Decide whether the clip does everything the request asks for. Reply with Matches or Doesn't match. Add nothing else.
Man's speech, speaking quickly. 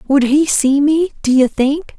Doesn't match